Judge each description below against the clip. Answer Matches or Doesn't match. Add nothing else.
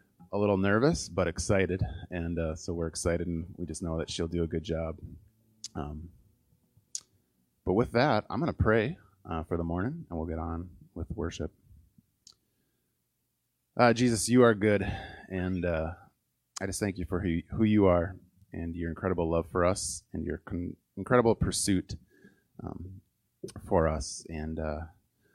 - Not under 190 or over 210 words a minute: Doesn't match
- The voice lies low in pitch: Matches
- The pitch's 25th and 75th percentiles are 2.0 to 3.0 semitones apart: Doesn't match